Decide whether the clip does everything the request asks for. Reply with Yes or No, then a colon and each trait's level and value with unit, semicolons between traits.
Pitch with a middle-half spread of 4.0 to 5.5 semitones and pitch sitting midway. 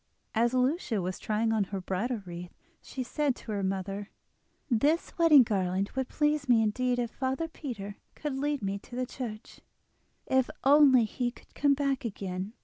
No: average, 5.2 semitones; high, 240 Hz